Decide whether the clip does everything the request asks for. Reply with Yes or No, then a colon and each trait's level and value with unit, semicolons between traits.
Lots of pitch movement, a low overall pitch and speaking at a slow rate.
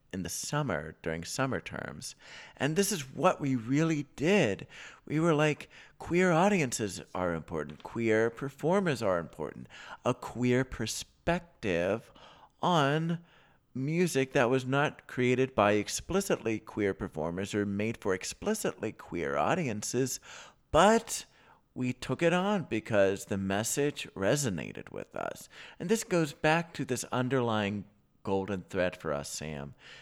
Yes: wide, 7.4 semitones; low, 125 Hz; slow, 130 wpm